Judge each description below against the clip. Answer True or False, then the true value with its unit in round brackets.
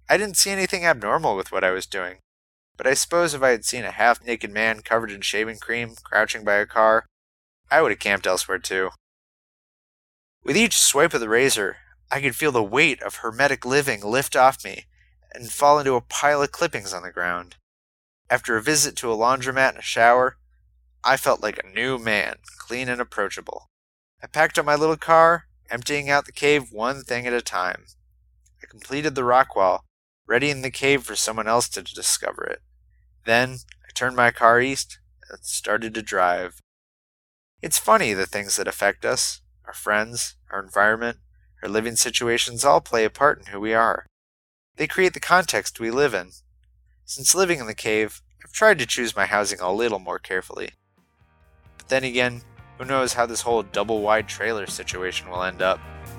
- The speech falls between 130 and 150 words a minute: False (190 wpm)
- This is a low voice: True (115 Hz)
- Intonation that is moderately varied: False (6.1 semitones)